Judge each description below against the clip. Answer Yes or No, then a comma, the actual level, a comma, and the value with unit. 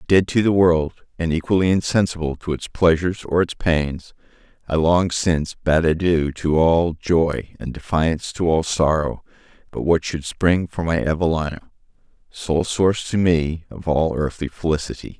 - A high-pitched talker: No, very low, 80 Hz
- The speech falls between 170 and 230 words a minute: No, average, 160 wpm